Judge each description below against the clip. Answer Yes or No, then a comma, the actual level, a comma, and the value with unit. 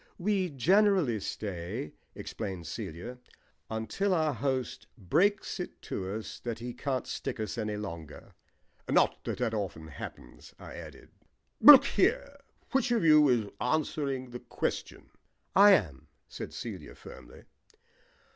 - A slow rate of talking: Yes, slow, 130 wpm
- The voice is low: Yes, low, 125 Hz